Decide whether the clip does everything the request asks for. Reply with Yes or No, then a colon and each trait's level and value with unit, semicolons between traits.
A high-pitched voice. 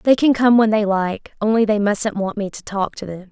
Yes: high, 210 Hz